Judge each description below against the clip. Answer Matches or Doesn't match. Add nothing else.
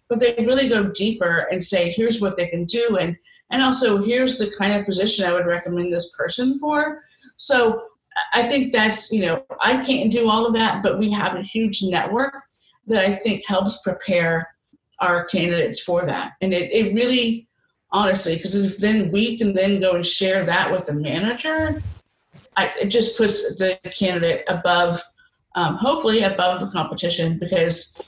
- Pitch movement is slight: Doesn't match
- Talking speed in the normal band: Matches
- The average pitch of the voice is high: Matches